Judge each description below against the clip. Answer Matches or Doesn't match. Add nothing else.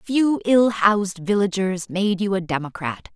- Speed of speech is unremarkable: Matches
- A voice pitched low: Doesn't match